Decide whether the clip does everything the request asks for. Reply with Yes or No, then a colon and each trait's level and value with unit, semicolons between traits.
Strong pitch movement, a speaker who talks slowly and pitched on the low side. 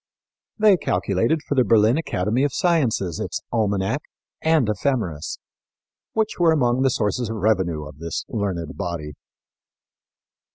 Yes: wide, 6.9 semitones; slow, 130 wpm; low, 110 Hz